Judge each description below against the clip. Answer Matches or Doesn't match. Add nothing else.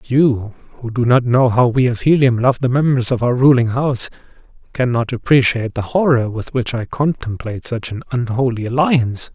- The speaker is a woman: Doesn't match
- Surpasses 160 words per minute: Matches